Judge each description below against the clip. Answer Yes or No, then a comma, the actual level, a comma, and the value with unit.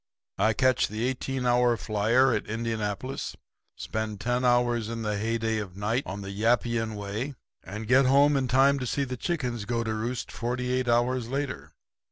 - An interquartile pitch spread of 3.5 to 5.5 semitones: No, average, 2.7 semitones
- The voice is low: Yes, low, 120 Hz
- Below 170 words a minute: No, average, 180 wpm